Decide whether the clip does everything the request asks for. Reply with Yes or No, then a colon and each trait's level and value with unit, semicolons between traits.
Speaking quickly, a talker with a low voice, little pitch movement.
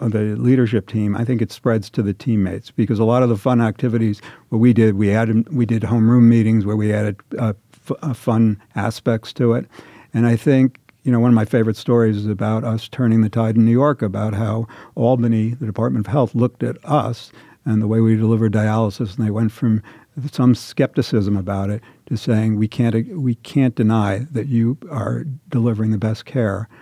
Yes: fast, 210 wpm; low, 115 Hz; narrow, 2.0 semitones